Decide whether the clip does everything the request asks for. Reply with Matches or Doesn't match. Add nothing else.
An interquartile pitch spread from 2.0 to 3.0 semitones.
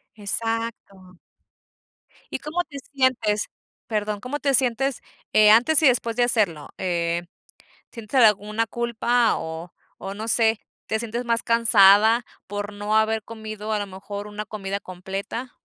Matches